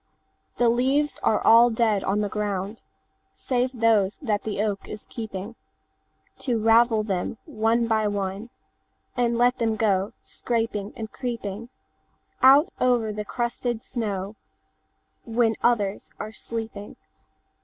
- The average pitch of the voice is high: Yes, high, 225 Hz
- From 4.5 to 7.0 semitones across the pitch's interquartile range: No, narrow, 2.4 semitones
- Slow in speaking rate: Yes, slow, 110 wpm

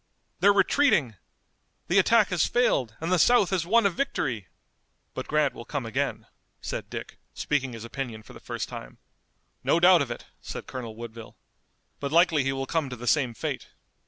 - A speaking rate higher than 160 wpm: Yes, average, 185 wpm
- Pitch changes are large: Yes, wide, 7.4 semitones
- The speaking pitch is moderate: Yes, medium, 145 Hz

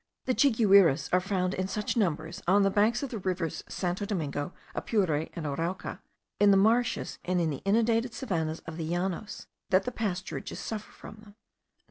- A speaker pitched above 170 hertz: Yes, high, 190 Hz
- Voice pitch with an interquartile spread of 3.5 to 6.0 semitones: Yes, average, 4.0 semitones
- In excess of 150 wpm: Yes, average, 175 wpm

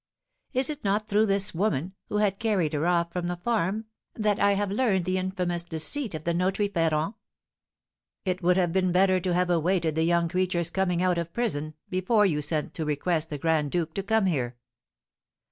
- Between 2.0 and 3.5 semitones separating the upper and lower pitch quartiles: Yes, average, 3.1 semitones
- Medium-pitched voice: Yes, medium, 180 Hz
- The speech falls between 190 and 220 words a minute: Yes, average, 195 wpm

